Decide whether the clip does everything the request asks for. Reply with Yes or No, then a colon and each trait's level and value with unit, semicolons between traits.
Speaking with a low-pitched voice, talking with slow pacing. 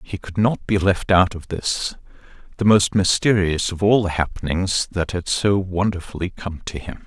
No: very low, 95 Hz; average, 185 wpm